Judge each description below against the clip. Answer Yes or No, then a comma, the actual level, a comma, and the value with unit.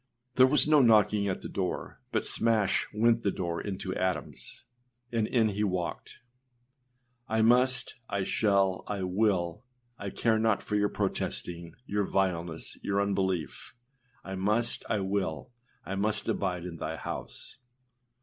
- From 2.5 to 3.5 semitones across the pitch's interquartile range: Yes, average, 3.0 semitones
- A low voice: Yes, low, 100 Hz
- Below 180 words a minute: Yes, average, 150 wpm